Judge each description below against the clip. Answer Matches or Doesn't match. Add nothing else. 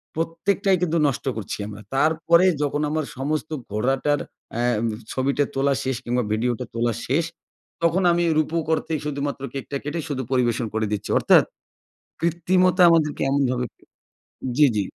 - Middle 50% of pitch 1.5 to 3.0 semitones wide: Doesn't match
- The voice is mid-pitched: Matches